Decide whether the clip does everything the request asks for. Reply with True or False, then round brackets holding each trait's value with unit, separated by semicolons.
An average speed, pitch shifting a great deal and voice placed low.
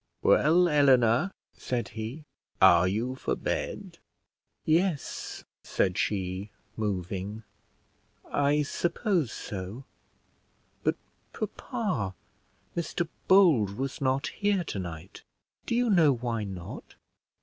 False (95 wpm; 8.5 semitones; 125 Hz)